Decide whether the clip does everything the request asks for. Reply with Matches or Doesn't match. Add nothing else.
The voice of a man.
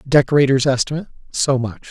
Matches